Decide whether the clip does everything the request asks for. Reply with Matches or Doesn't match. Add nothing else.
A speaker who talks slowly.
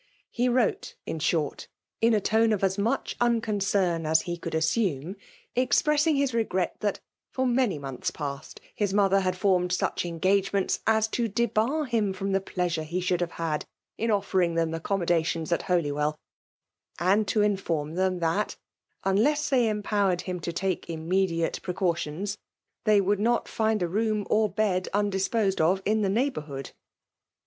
Doesn't match